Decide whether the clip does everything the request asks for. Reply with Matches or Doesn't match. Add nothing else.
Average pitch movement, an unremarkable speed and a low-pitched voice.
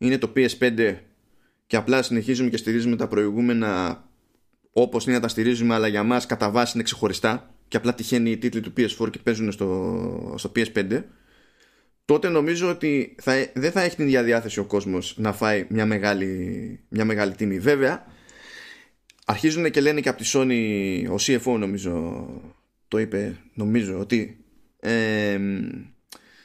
Matches